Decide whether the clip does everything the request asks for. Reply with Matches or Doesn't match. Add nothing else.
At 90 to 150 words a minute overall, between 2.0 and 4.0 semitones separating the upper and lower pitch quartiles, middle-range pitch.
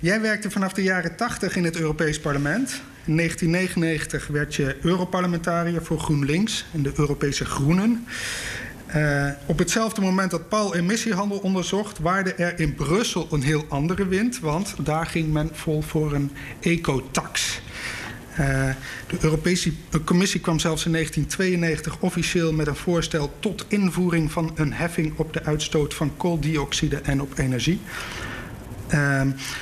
Matches